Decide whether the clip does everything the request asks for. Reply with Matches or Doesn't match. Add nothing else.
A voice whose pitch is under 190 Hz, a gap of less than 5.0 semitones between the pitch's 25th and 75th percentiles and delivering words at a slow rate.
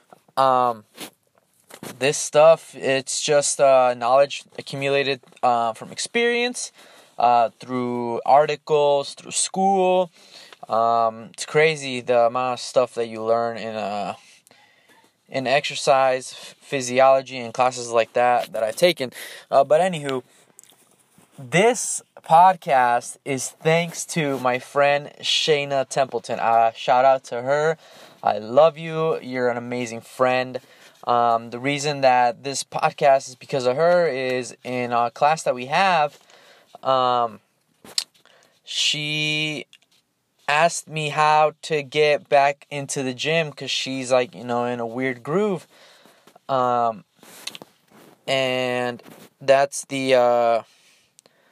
Matches